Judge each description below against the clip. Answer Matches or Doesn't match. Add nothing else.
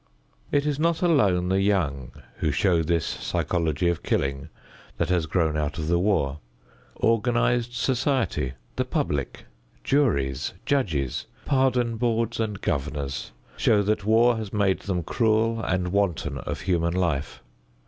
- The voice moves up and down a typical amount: Doesn't match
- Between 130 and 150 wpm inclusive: Matches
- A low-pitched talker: Matches